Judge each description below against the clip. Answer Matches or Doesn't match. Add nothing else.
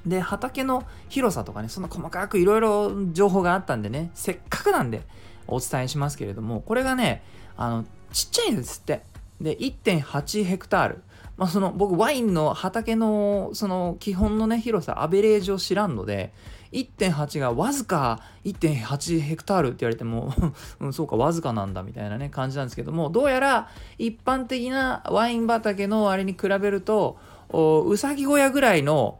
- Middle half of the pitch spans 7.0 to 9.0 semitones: Matches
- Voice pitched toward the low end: Doesn't match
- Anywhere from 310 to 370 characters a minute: Matches